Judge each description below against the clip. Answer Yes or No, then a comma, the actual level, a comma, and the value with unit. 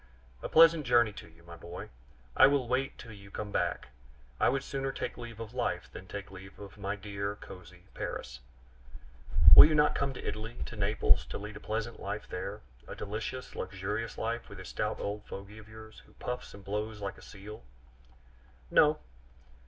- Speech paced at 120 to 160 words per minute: No, average, 190 wpm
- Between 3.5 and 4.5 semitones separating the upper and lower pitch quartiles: No, average, 3.1 semitones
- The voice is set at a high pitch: No, low, 105 Hz